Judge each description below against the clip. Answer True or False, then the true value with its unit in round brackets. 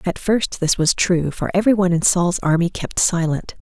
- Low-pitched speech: False (180 Hz)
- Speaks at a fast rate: True (215 wpm)